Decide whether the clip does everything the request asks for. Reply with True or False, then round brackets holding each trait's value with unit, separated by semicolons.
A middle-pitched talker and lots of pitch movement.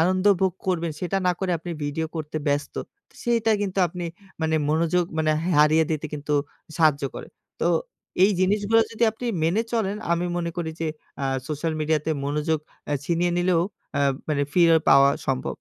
False (165 Hz; 3.2 semitones)